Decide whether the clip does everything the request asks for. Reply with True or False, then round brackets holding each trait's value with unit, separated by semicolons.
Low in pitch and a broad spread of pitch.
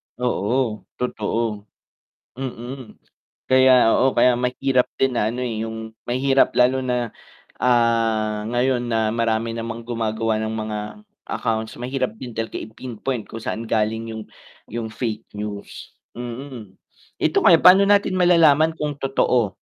False (120 Hz; 2.7 semitones)